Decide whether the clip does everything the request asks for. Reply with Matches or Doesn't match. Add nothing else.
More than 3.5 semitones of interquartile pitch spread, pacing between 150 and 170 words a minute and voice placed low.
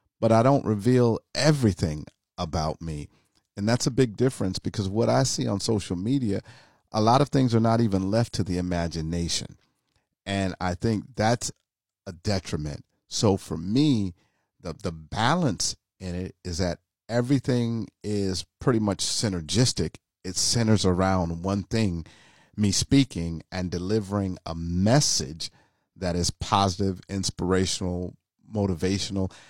Doesn't match